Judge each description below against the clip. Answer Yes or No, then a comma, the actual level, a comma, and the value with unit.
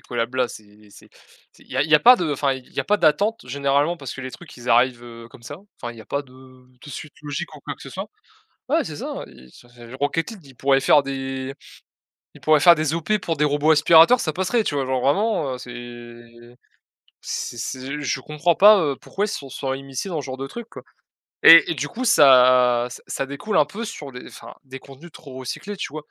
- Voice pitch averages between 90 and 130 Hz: No, medium, 140 Hz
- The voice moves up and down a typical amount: Yes, average, 3.8 semitones